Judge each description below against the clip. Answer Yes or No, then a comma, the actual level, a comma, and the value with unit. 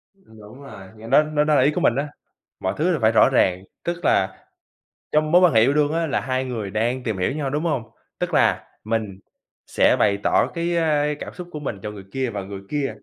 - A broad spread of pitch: Yes, wide, 5.9 semitones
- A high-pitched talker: No, low, 130 Hz